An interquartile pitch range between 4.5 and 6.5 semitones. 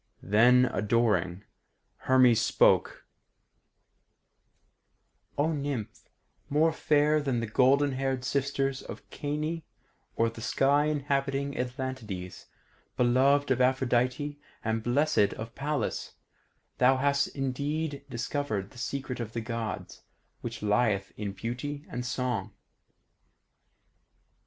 No: average, 3.5 semitones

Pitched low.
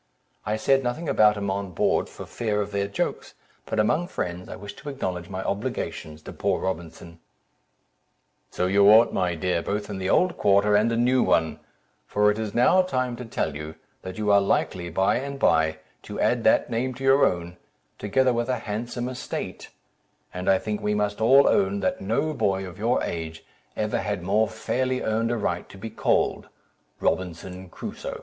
Yes: low, 105 Hz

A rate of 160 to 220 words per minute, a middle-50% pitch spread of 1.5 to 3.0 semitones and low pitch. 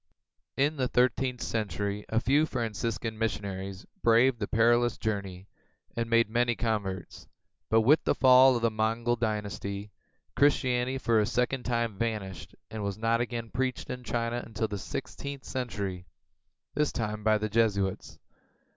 No: average, 145 wpm; average, 2.7 semitones; low, 115 Hz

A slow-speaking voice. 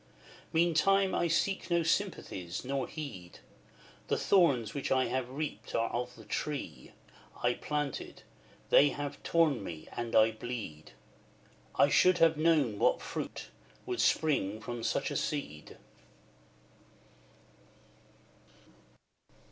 Yes: slow, 115 wpm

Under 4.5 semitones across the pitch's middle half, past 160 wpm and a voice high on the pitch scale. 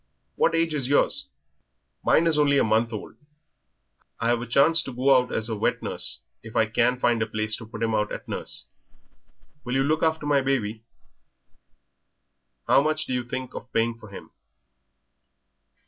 No: average, 4.0 semitones; average, 175 wpm; low, 125 Hz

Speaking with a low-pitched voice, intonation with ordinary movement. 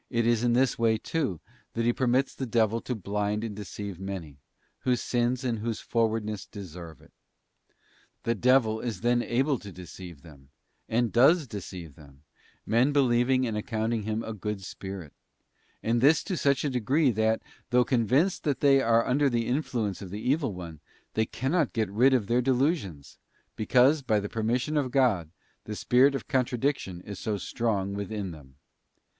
Yes: low, 115 Hz; average, 4.0 semitones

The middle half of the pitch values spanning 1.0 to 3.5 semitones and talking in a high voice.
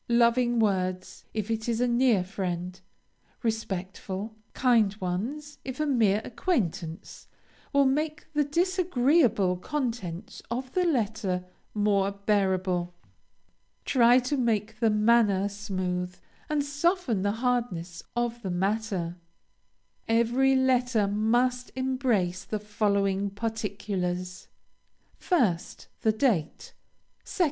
No: average, 4.6 semitones; high, 220 Hz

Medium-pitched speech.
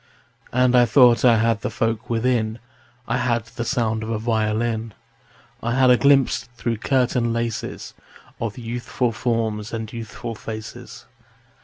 No: low, 115 Hz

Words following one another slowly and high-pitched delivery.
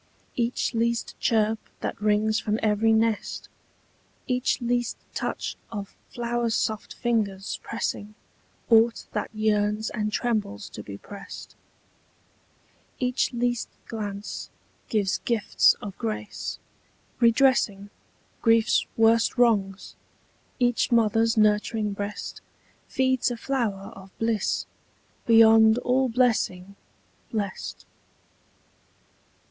Yes: slow, 100 wpm; high, 220 Hz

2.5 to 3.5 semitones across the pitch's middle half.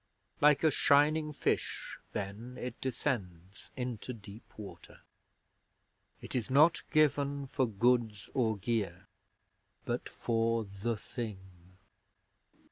No: average, 4.8 semitones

